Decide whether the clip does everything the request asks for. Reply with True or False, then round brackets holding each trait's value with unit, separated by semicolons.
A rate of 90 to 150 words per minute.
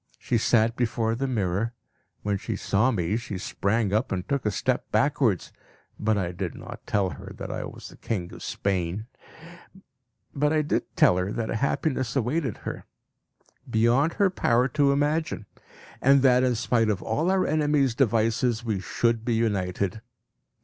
False (165 wpm)